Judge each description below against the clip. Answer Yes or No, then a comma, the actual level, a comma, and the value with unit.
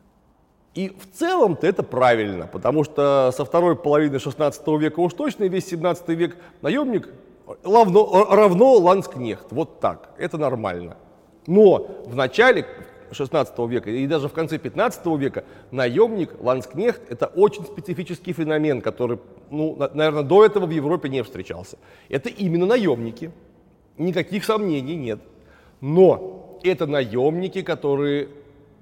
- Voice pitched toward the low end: No, medium, 155 Hz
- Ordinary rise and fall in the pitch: Yes, average, 5.0 semitones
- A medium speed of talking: Yes, average, 125 wpm